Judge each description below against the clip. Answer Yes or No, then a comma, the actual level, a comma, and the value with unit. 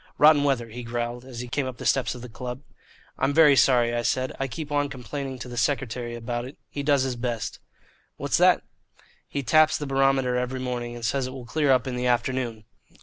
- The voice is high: No, low, 125 Hz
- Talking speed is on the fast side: Yes, fast, 220 wpm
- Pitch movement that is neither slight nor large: No, narrow, 2.2 semitones